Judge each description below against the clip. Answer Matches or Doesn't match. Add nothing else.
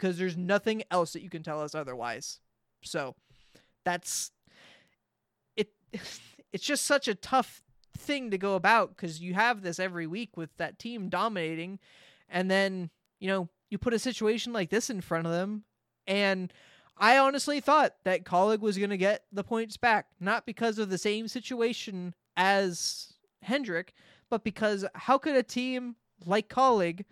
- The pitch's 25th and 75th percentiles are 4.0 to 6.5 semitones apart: Matches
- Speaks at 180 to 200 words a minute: Doesn't match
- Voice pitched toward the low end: Doesn't match